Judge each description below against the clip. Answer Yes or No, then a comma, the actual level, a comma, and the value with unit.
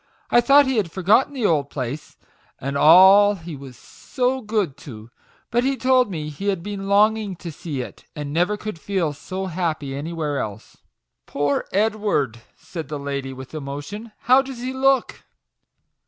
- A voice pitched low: No, medium, 175 Hz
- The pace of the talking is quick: No, average, 175 wpm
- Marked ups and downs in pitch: Yes, wide, 7.1 semitones